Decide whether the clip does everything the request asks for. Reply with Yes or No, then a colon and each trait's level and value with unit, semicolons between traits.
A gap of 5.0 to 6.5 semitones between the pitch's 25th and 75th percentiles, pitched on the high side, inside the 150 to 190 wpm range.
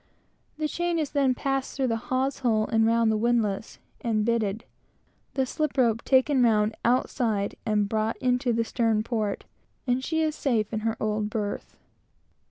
No: average, 3.3 semitones; high, 230 Hz; average, 170 wpm